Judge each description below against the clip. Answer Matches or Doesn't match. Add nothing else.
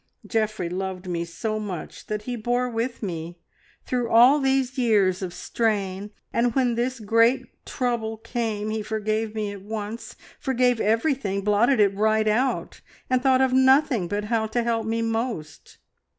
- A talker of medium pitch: Doesn't match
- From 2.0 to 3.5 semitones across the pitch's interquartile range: Matches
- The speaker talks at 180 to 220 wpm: Doesn't match